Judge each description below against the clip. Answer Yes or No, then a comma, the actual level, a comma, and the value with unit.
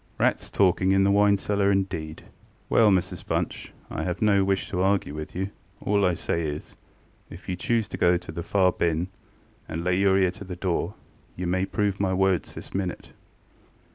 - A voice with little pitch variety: Yes, narrow, 1.9 semitones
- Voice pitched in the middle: No, very low, 95 Hz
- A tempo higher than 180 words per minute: Yes, average, 190 wpm